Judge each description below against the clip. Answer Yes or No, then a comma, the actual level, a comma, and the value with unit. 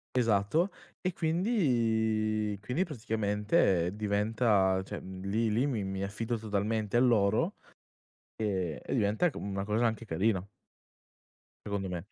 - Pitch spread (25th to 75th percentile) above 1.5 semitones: Yes, average, 2.8 semitones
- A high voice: No, low, 110 Hz